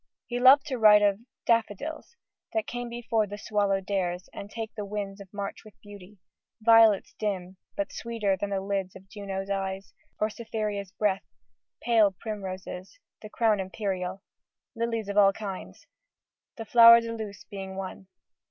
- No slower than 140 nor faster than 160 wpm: Yes, average, 155 wpm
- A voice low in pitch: No, high, 205 Hz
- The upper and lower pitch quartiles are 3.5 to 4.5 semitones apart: No, narrow, 2.4 semitones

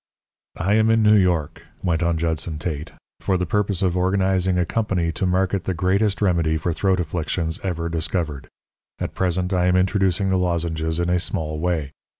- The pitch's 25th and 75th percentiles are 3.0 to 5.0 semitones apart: No, narrow, 2.5 semitones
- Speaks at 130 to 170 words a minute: No, average, 180 wpm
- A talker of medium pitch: No, very low, 90 Hz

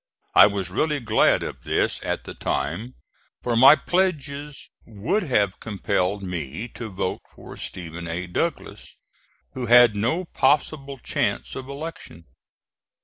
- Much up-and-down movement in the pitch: Yes, wide, 7.1 semitones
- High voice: No, low, 115 Hz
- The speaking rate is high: No, slow, 135 wpm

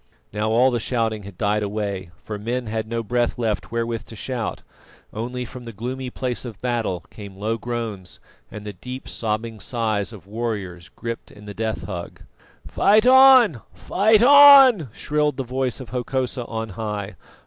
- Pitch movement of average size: Yes, average, 3.2 semitones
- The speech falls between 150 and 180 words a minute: Yes, average, 170 wpm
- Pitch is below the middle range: Yes, low, 115 Hz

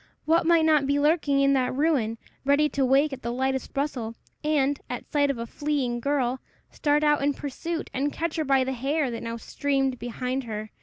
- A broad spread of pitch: No, average, 2.8 semitones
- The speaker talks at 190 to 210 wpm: Yes, fast, 205 wpm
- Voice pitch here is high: Yes, very high, 275 Hz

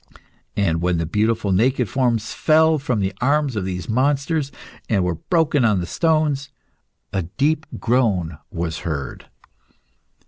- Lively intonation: Yes, wide, 7.7 semitones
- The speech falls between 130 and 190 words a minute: Yes, average, 140 wpm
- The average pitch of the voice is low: Yes, low, 115 Hz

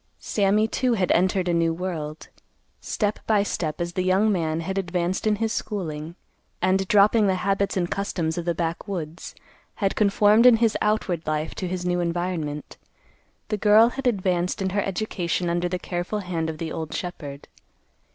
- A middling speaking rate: Yes, average, 175 wpm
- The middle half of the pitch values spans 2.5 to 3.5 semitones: Yes, average, 3.1 semitones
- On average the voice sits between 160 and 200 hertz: Yes, medium, 185 Hz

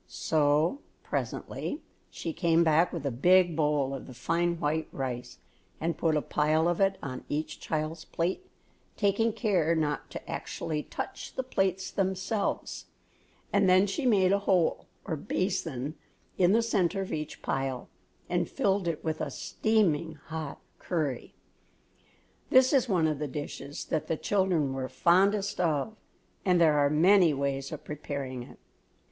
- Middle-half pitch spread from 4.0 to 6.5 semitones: Yes, average, 4.4 semitones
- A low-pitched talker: No, medium, 165 Hz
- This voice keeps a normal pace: Yes, average, 155 wpm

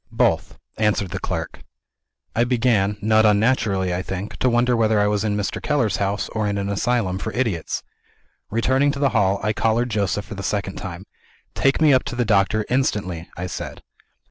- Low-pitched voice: Yes, low, 105 Hz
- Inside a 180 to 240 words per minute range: Yes, average, 190 wpm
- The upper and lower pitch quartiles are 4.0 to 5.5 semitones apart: No, average, 3.5 semitones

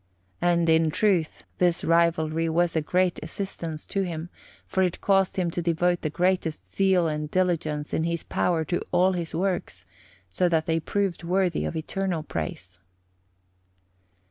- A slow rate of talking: No, average, 155 wpm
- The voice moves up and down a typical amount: No, narrow, 2.2 semitones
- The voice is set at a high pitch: No, medium, 170 Hz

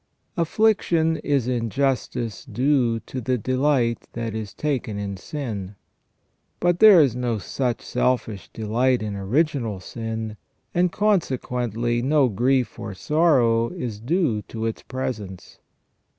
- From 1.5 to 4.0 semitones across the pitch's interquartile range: No, average, 4.4 semitones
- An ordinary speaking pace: No, slow, 125 wpm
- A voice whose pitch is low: Yes, low, 125 Hz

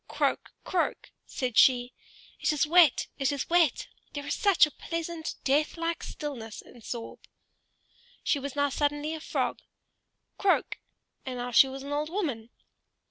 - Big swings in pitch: No, average, 3.7 semitones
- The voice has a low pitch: No, very high, 290 Hz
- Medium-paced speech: Yes, average, 150 wpm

